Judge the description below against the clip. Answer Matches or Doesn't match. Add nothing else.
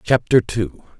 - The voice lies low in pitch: Matches